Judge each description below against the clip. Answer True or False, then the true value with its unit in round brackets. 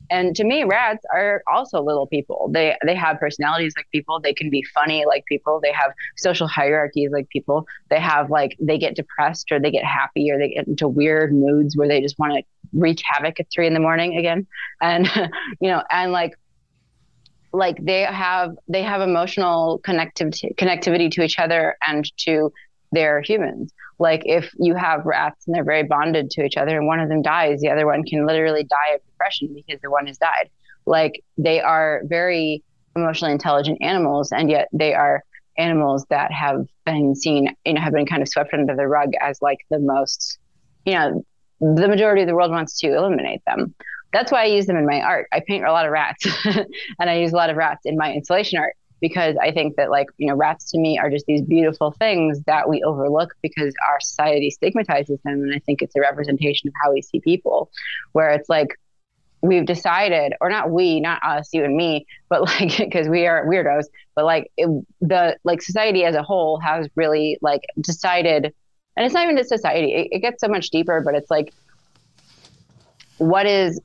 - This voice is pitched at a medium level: True (155 Hz)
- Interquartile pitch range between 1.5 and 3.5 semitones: True (2.8 semitones)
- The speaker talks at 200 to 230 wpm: True (205 wpm)